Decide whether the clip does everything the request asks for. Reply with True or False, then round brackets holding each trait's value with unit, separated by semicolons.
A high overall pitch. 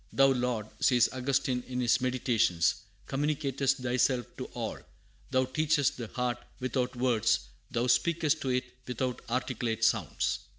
False (125 Hz)